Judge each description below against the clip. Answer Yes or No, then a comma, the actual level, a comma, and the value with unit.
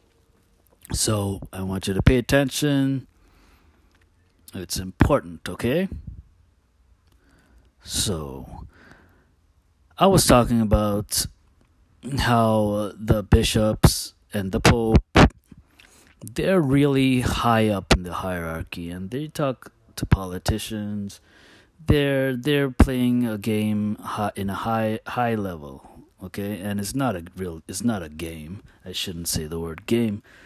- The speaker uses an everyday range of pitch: Yes, average, 4.7 semitones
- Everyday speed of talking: No, slow, 115 wpm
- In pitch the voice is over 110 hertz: No, low, 100 Hz